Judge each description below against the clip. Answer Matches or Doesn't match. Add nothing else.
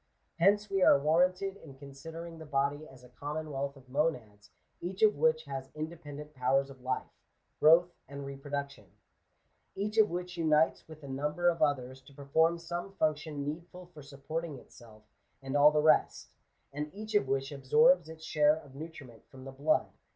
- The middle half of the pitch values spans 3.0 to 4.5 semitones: Matches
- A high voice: Doesn't match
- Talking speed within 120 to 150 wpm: Doesn't match